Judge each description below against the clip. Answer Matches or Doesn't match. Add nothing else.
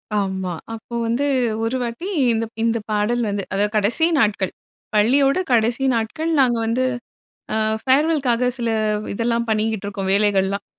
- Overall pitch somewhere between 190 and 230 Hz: Matches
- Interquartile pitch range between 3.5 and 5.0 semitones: Doesn't match